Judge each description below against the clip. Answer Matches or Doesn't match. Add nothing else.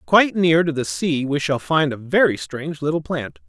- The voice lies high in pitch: Doesn't match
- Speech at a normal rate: Doesn't match